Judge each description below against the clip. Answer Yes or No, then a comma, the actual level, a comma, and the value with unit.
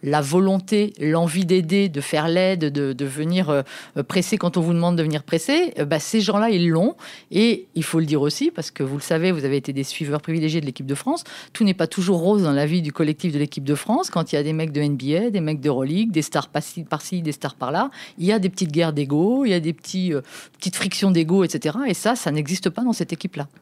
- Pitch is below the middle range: No, medium, 165 Hz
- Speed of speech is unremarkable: No, fast, 265 wpm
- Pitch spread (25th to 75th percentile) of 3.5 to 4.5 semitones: Yes, average, 4.2 semitones